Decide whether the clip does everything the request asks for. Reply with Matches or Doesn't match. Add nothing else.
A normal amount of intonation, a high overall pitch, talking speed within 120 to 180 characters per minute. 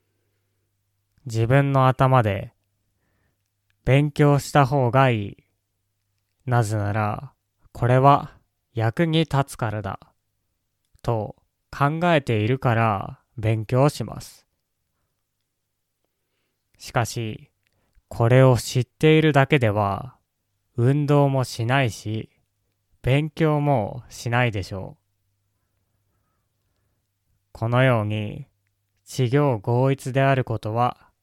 Doesn't match